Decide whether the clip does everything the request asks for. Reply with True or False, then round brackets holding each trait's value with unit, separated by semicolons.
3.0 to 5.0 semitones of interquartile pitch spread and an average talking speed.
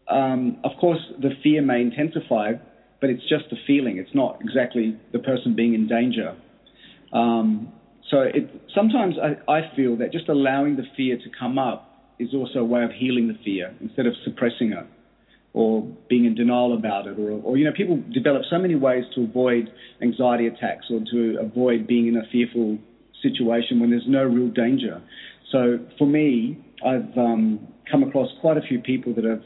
True (4.1 semitones; 185 wpm)